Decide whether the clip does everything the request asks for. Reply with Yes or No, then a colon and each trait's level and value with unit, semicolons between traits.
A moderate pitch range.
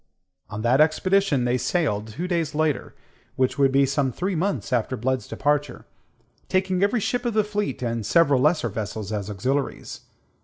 No: wide, 6.6 semitones